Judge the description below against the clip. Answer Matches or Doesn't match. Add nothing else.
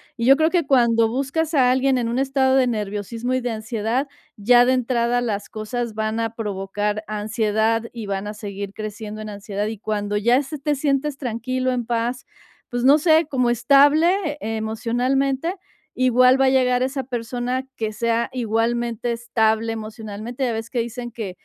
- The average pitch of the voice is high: Matches